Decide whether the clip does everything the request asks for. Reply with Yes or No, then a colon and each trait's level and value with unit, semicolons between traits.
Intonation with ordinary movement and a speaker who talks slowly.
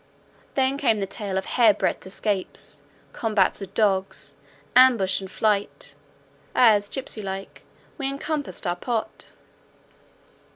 Yes: average, 4.4 semitones; slow, 120 wpm